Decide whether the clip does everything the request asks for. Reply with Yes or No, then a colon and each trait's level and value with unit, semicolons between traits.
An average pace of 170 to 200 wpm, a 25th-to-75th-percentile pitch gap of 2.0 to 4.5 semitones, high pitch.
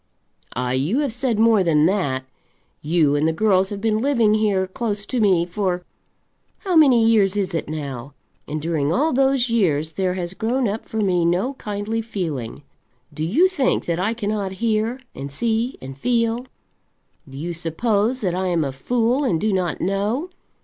No: average, 180 wpm; wide, 5.5 semitones; high, 200 Hz